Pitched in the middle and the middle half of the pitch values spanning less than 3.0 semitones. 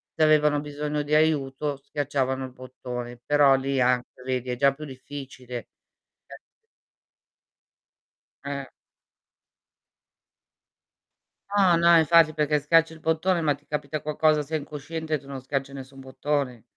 Yes: medium, 145 Hz; narrow, 2.6 semitones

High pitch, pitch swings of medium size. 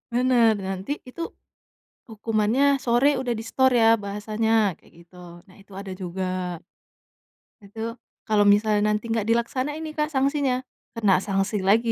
Yes: high, 225 Hz; average, 3.6 semitones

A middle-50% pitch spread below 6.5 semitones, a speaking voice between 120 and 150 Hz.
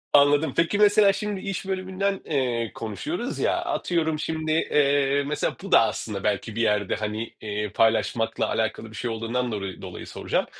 No: wide, 7.0 semitones; low, 135 Hz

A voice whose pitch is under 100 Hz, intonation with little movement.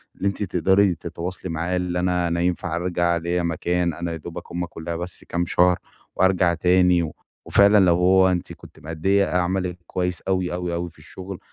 Yes: very low, 90 Hz; narrow, 1.2 semitones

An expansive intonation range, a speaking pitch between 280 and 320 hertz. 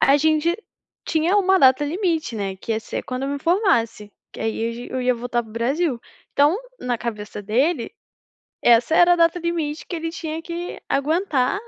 Yes: wide, 6.2 semitones; very high, 285 Hz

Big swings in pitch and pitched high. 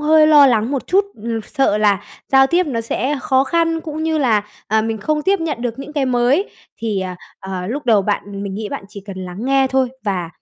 Yes: wide, 6.2 semitones; very high, 250 Hz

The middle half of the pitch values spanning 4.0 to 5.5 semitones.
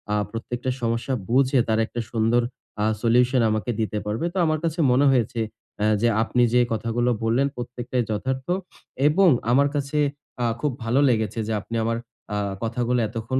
No: narrow, 2.5 semitones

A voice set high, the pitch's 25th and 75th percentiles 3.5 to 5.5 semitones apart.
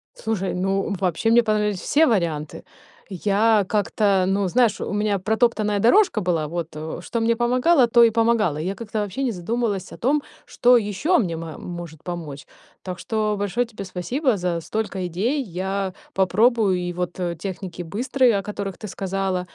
Yes: high, 200 Hz; average, 4.1 semitones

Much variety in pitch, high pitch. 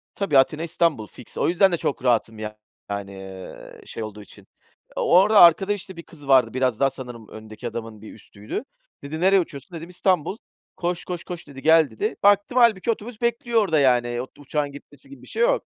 No: wide, 8.1 semitones; medium, 150 Hz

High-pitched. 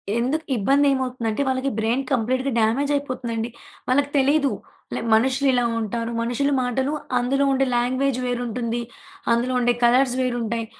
Yes: very high, 250 Hz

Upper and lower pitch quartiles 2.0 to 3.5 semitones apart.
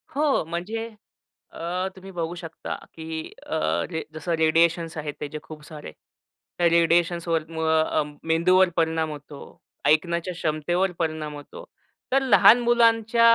Yes: average, 2.7 semitones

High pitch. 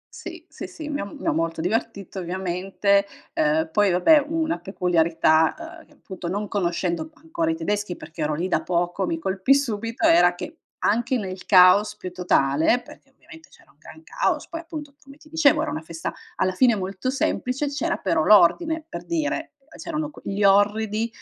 Yes: high, 200 Hz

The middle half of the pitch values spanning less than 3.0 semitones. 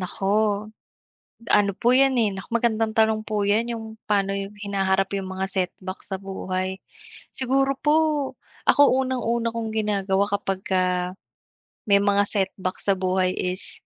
Yes: narrow, 2.6 semitones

